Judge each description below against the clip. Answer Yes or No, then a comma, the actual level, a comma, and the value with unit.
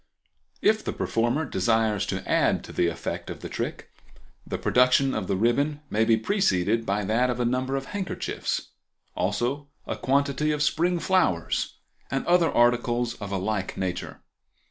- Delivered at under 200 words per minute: Yes, average, 165 wpm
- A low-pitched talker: Yes, low, 120 Hz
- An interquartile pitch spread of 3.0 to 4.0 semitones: No, average, 5.2 semitones